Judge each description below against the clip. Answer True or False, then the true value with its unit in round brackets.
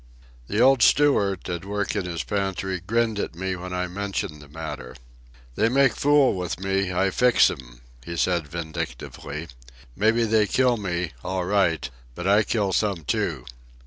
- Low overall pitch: True (95 Hz)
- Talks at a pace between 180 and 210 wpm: False (165 wpm)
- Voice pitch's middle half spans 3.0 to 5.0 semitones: True (3.7 semitones)